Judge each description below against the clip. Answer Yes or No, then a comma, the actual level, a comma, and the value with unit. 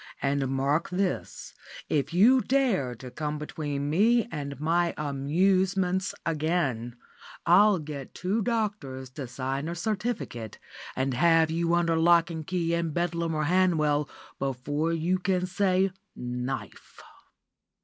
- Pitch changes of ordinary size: Yes, average, 4.7 semitones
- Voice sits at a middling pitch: Yes, medium, 165 Hz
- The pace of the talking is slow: Yes, slow, 130 wpm